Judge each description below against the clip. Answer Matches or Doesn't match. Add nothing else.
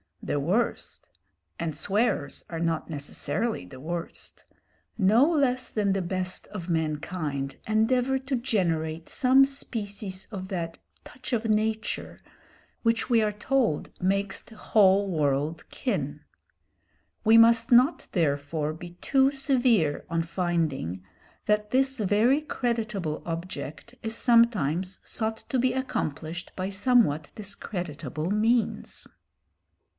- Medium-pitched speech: Doesn't match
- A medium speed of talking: Doesn't match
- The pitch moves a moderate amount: Doesn't match